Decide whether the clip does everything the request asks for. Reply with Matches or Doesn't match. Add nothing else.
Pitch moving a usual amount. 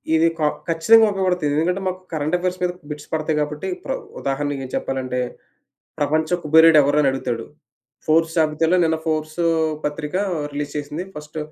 Doesn't match